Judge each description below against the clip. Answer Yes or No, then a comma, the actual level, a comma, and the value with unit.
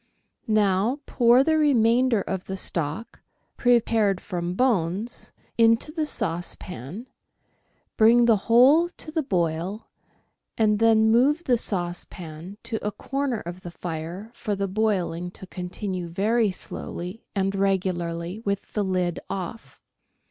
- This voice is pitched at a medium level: No, high, 205 Hz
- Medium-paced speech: No, slow, 125 wpm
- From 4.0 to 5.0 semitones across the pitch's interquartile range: Yes, average, 4.6 semitones